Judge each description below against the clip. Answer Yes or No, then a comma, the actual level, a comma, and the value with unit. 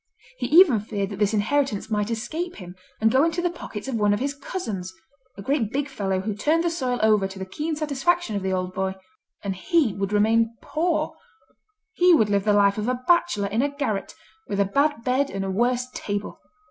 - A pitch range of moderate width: No, wide, 6.3 semitones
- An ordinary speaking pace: No, fast, 215 wpm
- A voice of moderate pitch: No, high, 225 Hz